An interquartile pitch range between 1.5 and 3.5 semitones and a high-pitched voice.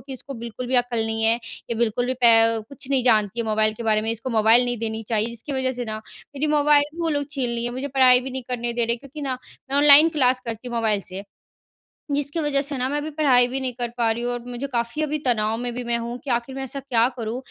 Yes: average, 2.8 semitones; high, 245 Hz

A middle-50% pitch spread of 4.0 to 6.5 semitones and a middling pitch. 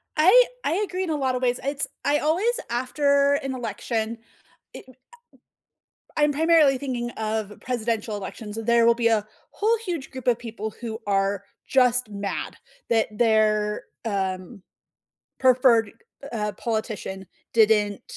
No: average, 4.4 semitones; high, 235 Hz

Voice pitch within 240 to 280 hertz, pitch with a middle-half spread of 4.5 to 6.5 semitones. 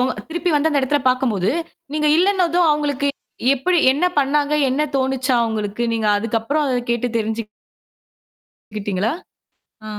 Yes: very high, 265 Hz; average, 4.8 semitones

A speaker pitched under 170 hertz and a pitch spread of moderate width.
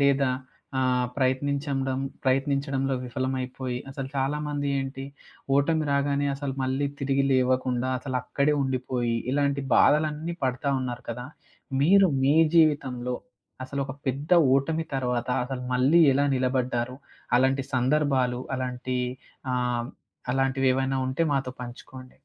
No: low, 135 Hz; narrow, 1.7 semitones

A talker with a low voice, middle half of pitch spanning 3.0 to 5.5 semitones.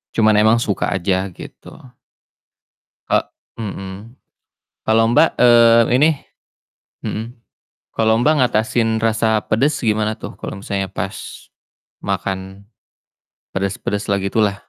No: low, 110 Hz; narrow, 2.5 semitones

